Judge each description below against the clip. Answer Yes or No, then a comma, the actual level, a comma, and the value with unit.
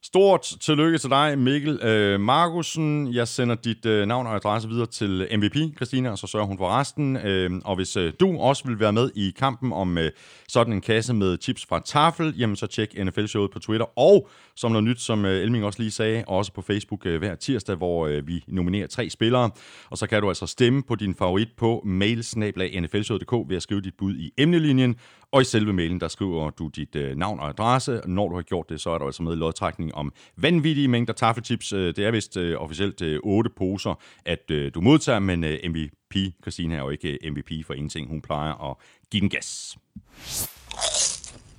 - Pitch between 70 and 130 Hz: Yes, low, 105 Hz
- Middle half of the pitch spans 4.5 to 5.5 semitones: Yes, average, 5.0 semitones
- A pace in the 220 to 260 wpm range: No, average, 200 wpm